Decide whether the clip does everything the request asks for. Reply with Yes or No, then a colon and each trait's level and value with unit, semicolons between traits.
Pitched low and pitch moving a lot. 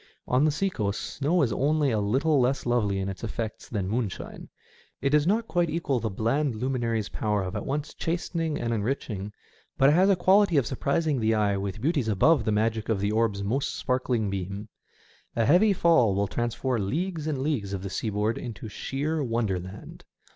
Yes: low, 120 Hz; wide, 6.1 semitones